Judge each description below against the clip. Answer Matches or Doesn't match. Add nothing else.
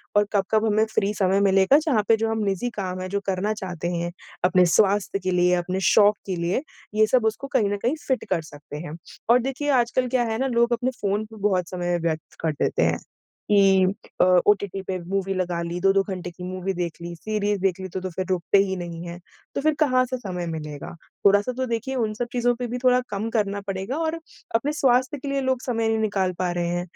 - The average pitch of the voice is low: Doesn't match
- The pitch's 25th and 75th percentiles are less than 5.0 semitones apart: Matches